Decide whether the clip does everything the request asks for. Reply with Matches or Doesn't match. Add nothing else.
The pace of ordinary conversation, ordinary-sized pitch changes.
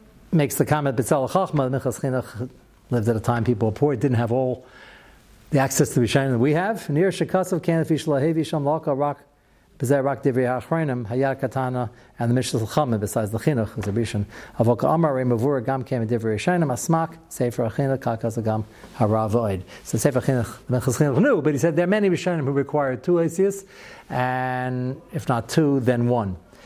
Matches